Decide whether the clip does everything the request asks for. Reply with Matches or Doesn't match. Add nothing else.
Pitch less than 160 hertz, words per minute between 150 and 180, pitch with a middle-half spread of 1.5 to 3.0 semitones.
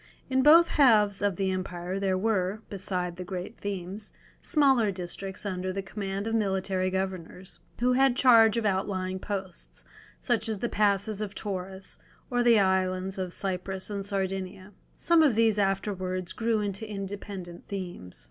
Doesn't match